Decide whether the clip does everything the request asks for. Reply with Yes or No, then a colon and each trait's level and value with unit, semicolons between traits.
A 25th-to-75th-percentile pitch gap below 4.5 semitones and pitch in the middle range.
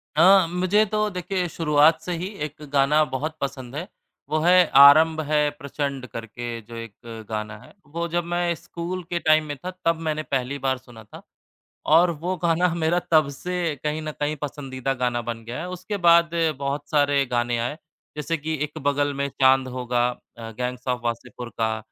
No: average, 5.0 semitones; medium, 150 Hz